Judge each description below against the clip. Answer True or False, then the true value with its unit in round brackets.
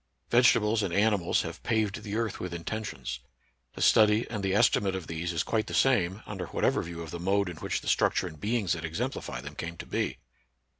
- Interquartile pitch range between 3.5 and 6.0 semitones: True (4.2 semitones)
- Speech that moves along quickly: True (215 wpm)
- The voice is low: True (95 Hz)